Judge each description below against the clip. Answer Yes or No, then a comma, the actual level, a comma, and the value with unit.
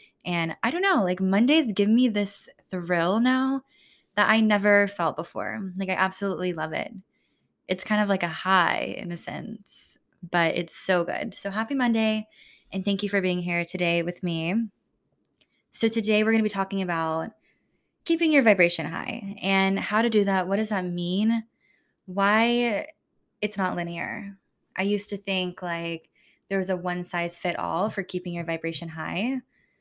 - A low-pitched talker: No, high, 195 Hz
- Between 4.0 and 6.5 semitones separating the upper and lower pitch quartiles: No, average, 3.5 semitones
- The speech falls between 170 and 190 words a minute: Yes, average, 175 wpm